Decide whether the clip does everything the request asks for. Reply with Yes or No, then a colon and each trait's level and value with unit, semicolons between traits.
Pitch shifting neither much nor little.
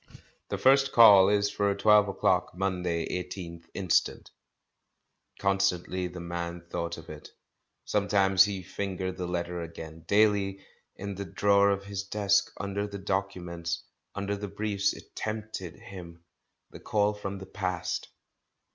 No: narrow, 2.3 semitones